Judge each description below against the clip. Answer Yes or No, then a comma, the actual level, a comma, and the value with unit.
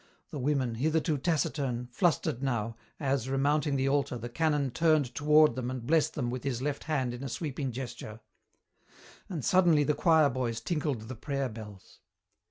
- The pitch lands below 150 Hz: Yes, low, 135 Hz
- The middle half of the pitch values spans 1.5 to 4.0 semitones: Yes, average, 3.6 semitones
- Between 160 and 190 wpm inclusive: Yes, average, 170 wpm